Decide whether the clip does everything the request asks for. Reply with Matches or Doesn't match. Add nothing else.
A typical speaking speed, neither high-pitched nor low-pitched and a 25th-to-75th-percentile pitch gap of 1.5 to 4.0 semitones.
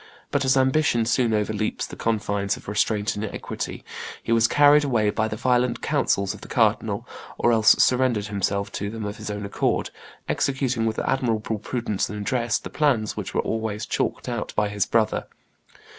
Doesn't match